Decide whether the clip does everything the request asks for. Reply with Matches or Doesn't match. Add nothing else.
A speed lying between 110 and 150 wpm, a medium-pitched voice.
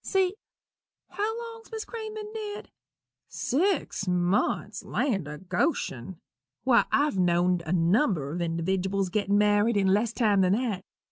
Doesn't match